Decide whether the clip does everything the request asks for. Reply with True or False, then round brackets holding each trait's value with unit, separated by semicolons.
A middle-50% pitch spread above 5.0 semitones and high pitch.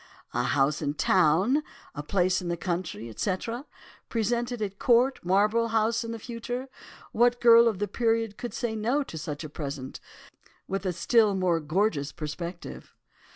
True (5.6 semitones; 200 Hz)